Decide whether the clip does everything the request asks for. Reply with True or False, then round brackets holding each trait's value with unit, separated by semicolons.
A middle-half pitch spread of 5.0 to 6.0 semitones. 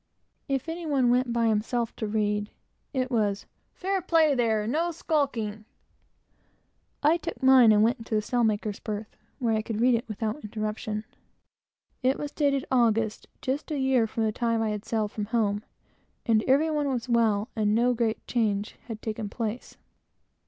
False (3.4 semitones)